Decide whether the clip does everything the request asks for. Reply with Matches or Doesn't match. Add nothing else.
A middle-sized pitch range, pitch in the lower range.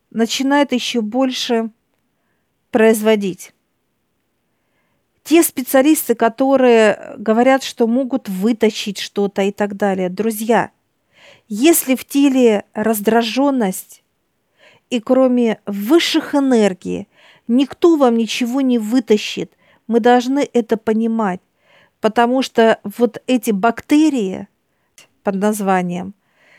Doesn't match